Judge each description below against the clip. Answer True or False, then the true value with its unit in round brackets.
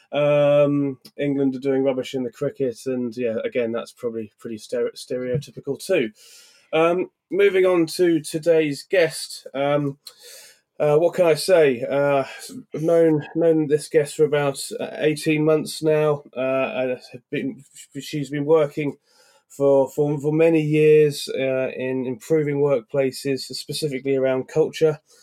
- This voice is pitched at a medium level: True (145 Hz)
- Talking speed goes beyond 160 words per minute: False (135 wpm)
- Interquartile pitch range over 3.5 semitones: False (2.6 semitones)